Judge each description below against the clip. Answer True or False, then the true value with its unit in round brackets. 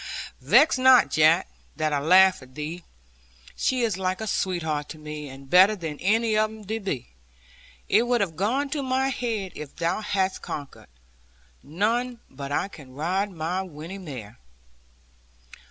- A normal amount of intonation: False (6.1 semitones)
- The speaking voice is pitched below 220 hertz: True (185 Hz)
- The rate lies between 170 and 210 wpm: False (155 wpm)